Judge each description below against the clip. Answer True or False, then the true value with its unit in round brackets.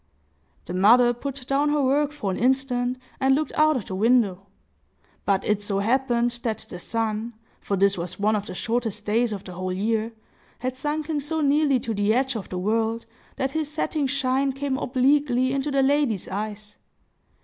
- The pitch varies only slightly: False (4.5 semitones)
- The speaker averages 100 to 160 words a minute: False (180 wpm)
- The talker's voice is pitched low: False (240 Hz)